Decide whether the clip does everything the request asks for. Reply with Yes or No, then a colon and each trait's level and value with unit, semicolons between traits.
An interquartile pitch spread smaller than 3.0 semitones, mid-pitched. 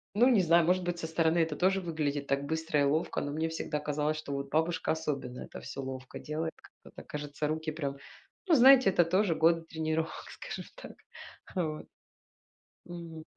Yes: narrow, 2.6 semitones; medium, 160 Hz